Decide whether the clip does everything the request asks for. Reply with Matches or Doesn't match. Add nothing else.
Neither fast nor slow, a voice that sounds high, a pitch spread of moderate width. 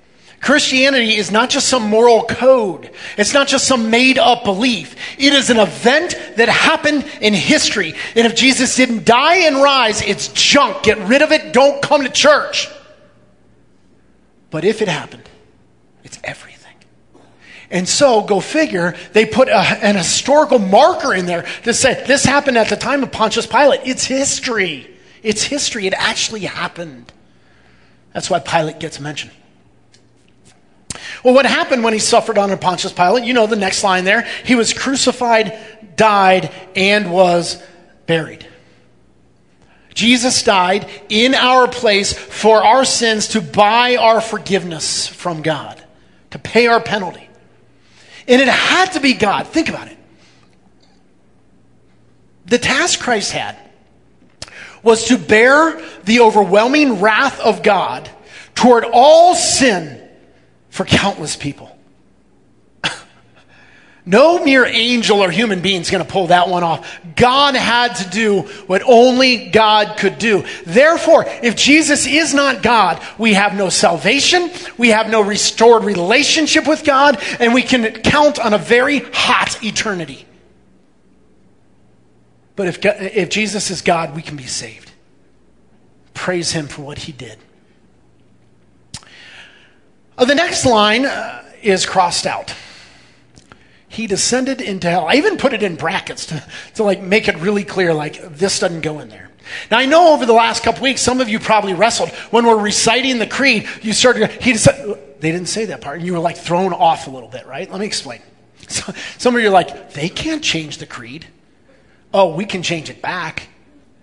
Doesn't match